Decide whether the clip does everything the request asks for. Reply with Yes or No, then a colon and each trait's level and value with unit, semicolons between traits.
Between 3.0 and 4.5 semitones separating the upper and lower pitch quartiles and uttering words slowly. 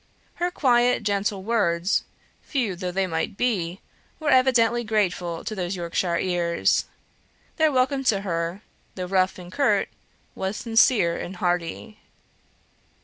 No: average, 5.2 semitones; slow, 130 wpm